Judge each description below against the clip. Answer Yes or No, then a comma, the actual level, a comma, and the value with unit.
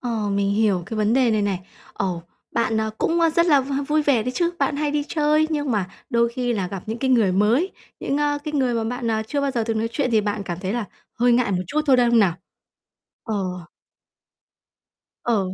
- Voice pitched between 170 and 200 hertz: No, high, 235 Hz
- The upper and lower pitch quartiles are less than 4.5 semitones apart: No, average, 5.2 semitones